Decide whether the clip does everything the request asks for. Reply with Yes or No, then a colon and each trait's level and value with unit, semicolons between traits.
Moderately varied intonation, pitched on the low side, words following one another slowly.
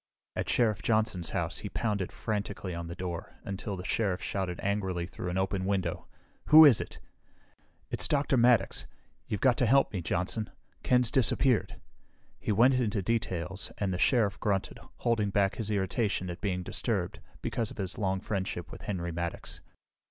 No: average, 3.6 semitones; low, 100 Hz; average, 165 wpm